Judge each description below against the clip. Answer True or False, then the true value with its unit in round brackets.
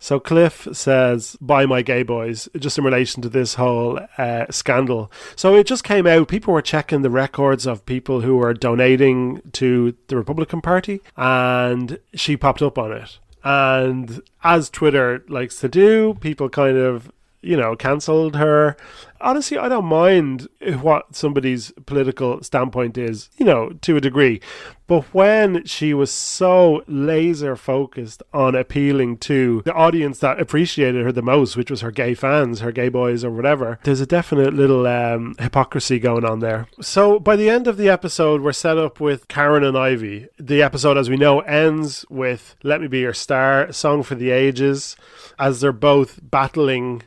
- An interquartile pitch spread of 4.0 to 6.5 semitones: False (3.5 semitones)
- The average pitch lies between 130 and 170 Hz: True (135 Hz)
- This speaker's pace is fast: False (175 wpm)